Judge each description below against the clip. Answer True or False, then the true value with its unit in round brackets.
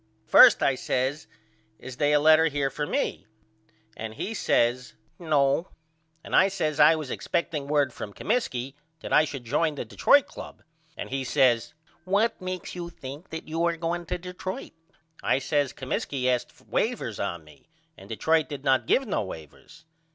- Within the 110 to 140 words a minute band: False (165 wpm)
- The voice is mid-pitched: True (145 Hz)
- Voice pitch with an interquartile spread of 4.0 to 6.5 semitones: True (4.3 semitones)